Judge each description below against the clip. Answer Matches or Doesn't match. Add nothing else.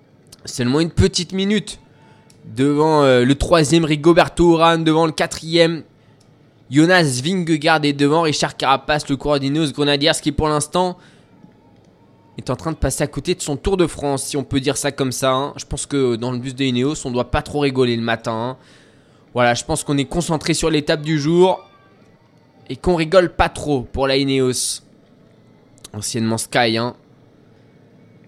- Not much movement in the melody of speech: Doesn't match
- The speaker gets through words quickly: Doesn't match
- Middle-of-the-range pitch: Matches